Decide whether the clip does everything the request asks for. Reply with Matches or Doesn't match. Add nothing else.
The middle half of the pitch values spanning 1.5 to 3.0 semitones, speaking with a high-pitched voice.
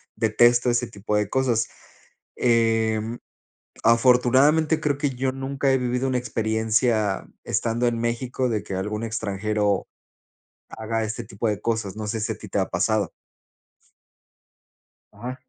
Doesn't match